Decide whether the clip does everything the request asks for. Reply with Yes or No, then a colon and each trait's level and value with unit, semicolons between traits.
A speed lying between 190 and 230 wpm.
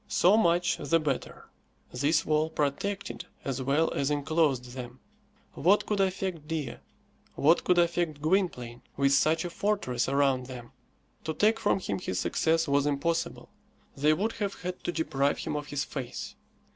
No: average, 160 wpm